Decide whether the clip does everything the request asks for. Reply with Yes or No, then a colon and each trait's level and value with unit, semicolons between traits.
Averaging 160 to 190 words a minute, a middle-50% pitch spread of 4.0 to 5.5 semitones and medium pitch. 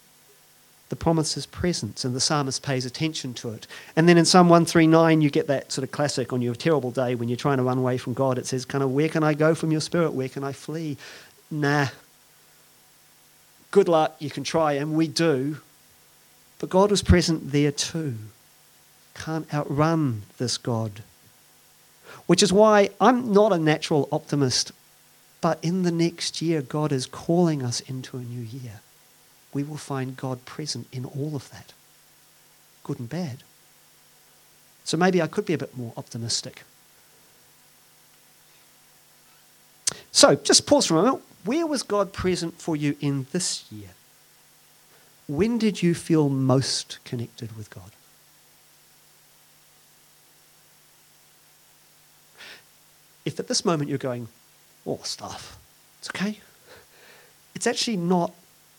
No: average, 150 wpm; average, 4.8 semitones; medium, 145 Hz